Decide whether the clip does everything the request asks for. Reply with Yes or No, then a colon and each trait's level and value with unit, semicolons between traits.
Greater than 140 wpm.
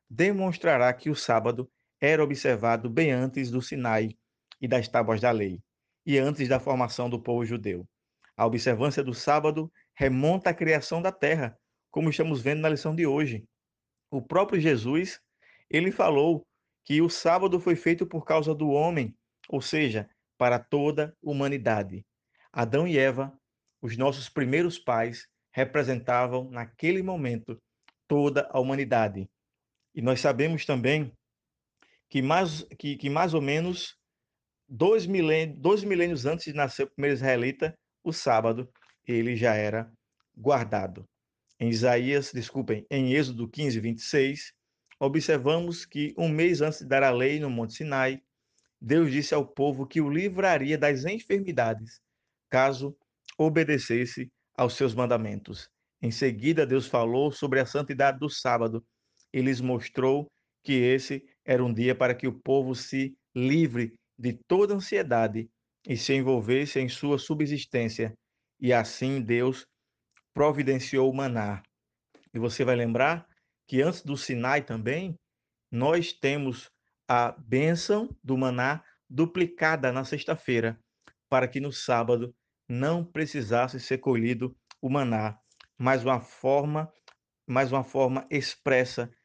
No: average, 135 wpm